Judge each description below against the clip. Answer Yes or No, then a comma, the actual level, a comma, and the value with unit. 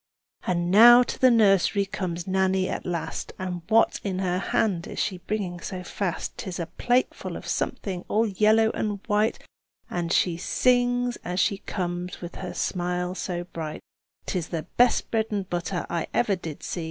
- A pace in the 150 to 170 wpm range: No, average, 180 wpm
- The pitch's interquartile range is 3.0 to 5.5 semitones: Yes, average, 3.4 semitones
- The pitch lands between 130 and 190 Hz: Yes, medium, 185 Hz